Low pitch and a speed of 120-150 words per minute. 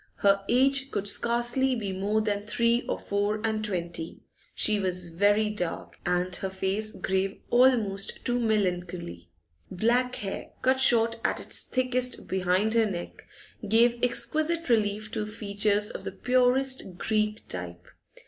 No: high, 215 Hz; average, 140 wpm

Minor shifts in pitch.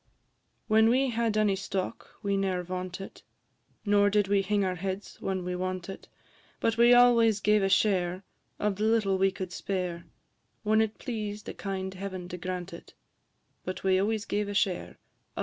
Yes: narrow, 2.3 semitones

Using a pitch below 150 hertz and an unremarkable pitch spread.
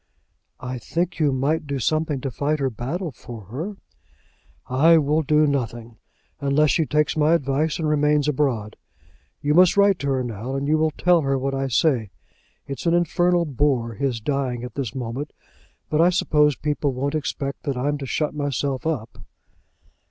Yes: medium, 140 Hz; average, 3.1 semitones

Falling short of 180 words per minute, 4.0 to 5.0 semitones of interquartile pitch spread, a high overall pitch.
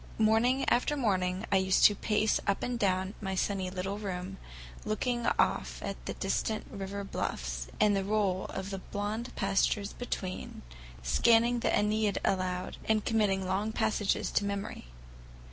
No: average, 150 wpm; narrow, 2.4 semitones; high, 200 Hz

